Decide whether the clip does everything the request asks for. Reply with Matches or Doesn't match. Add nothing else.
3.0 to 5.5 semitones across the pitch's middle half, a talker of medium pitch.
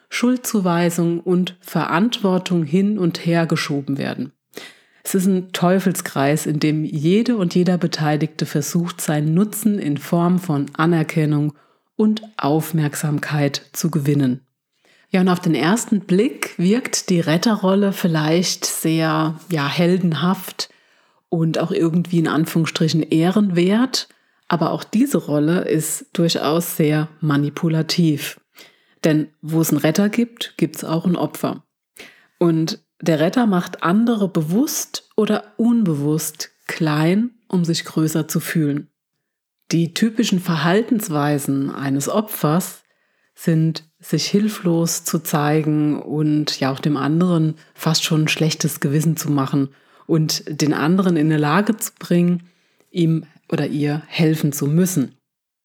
Matches